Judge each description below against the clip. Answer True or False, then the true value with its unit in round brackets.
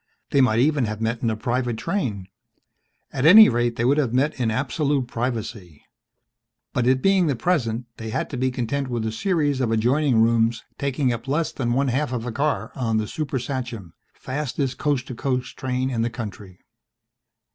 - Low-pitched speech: True (125 Hz)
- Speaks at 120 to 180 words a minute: False (190 wpm)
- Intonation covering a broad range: False (3.5 semitones)